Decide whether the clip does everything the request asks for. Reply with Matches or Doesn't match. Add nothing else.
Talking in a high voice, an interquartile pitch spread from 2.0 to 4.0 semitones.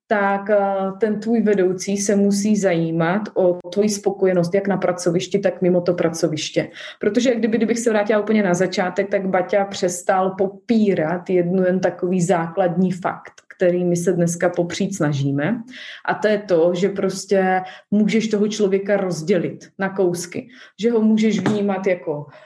Matches